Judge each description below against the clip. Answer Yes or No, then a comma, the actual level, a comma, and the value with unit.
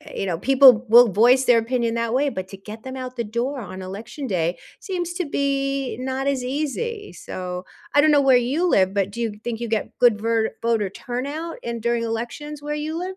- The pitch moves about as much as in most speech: Yes, average, 4.0 semitones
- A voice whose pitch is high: Yes, high, 245 Hz